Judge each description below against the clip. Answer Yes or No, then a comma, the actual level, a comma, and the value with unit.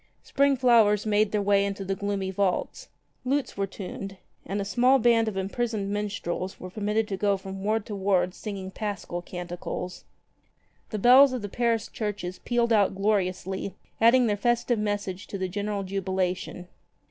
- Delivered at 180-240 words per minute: No, average, 165 wpm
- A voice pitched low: No, high, 205 Hz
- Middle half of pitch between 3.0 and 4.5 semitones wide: No, narrow, 2.5 semitones